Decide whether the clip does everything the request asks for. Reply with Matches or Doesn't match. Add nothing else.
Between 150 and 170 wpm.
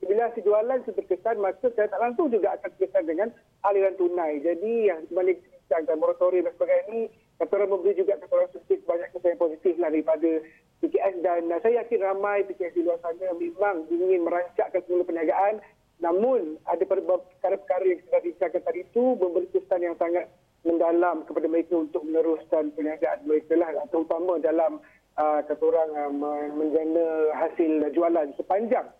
Matches